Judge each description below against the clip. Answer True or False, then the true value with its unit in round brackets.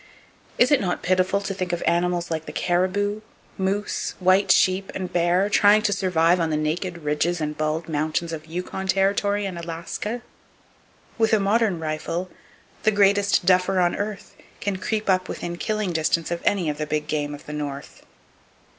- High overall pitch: False (180 Hz)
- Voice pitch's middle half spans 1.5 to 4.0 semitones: True (3.5 semitones)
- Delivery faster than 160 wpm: True (175 wpm)